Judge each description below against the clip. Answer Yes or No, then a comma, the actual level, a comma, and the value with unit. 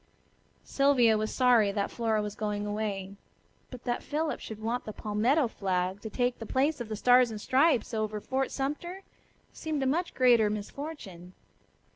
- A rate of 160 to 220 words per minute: Yes, average, 165 wpm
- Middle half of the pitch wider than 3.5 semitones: Yes, average, 4.2 semitones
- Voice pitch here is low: No, high, 230 Hz